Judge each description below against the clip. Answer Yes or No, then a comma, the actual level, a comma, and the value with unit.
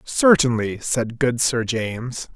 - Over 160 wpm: No, slow, 125 wpm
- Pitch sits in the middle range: No, low, 120 Hz